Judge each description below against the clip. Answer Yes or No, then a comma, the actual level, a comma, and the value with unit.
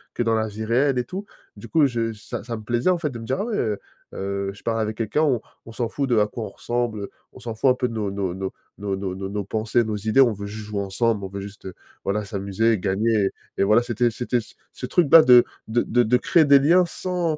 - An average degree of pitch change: Yes, average, 3.4 semitones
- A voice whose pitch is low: Yes, low, 115 Hz